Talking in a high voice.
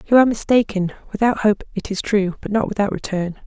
Yes: high, 205 Hz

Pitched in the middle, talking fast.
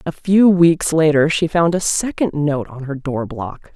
Yes: medium, 155 Hz; fast, 210 wpm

